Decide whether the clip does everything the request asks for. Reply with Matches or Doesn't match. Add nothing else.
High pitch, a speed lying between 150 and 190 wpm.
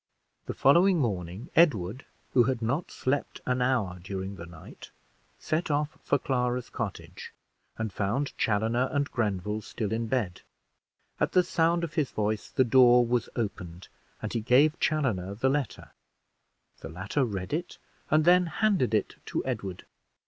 Doesn't match